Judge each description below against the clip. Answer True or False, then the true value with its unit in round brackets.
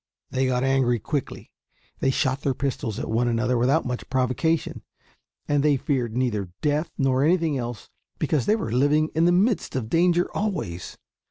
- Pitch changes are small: False (4.0 semitones)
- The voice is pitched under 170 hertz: True (135 Hz)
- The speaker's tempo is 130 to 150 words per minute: False (170 wpm)